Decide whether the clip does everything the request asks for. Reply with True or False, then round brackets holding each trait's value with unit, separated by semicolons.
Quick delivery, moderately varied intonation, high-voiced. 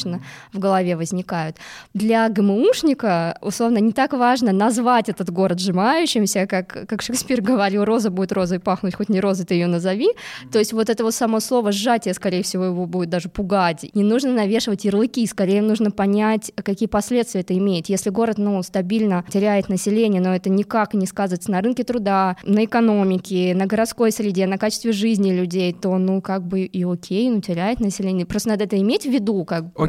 True (185 wpm; 3.0 semitones; 200 Hz)